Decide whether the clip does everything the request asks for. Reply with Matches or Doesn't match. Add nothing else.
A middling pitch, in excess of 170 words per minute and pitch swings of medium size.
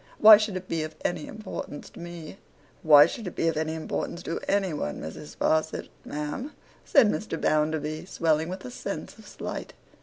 Matches